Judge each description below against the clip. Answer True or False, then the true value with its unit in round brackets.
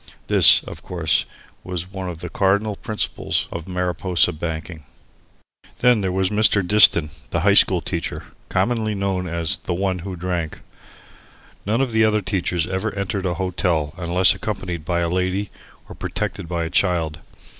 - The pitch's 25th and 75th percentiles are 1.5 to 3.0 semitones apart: True (2.6 semitones)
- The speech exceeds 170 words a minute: False (160 wpm)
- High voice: False (90 Hz)